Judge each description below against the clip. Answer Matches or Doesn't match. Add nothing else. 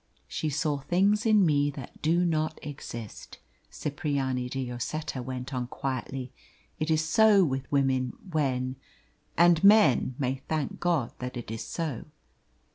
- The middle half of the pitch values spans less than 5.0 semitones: Matches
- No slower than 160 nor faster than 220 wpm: Doesn't match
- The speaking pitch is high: Doesn't match